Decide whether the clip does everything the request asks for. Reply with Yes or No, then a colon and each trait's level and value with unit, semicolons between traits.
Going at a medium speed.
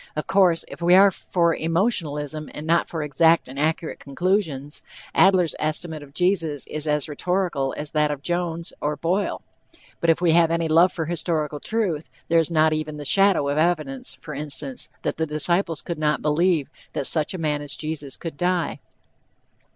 Yes: average, 180 wpm